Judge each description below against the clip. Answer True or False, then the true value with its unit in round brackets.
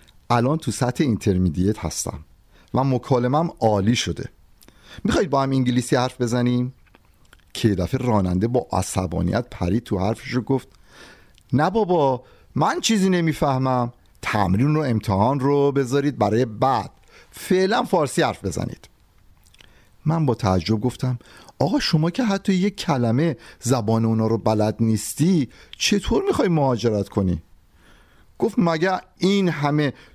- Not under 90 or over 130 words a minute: True (125 wpm)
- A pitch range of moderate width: False (6.4 semitones)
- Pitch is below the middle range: True (125 Hz)